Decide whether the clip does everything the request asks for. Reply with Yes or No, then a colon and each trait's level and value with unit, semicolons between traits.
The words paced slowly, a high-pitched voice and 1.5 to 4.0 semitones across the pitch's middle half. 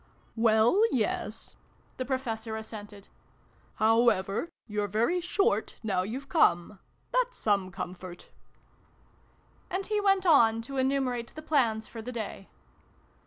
No: slow, 130 wpm; high, 230 Hz; average, 4.8 semitones